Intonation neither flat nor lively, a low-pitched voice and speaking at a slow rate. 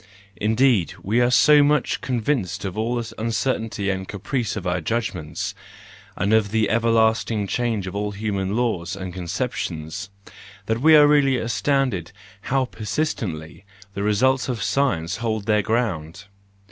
No: average, 4.2 semitones; low, 110 Hz; average, 145 wpm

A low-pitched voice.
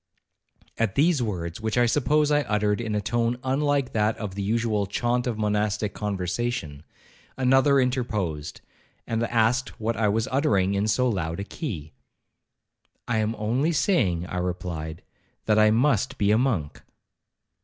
Yes: low, 110 Hz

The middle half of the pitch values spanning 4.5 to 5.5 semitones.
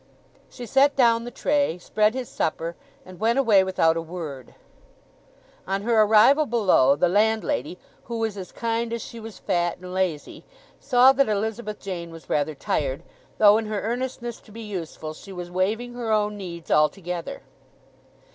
Yes: average, 4.9 semitones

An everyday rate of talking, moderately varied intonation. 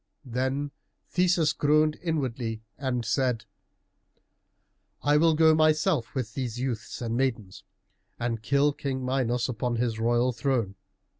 No: slow, 125 wpm; average, 3.7 semitones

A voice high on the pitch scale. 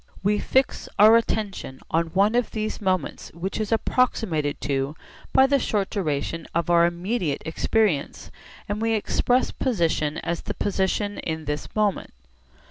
Yes: high, 195 Hz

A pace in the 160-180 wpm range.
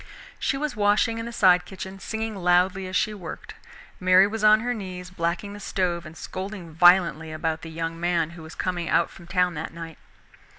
No: average, 200 wpm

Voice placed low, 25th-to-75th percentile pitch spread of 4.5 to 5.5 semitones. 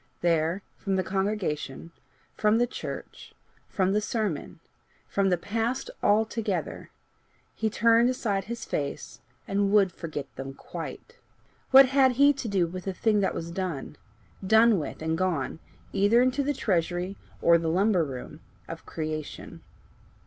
No: high, 195 Hz; average, 5.1 semitones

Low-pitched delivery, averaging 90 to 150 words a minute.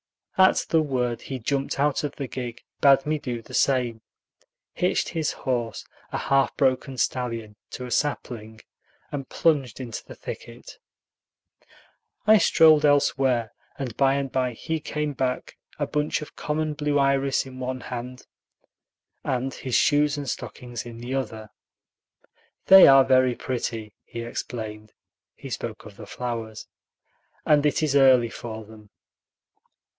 Yes: low, 130 Hz; average, 145 wpm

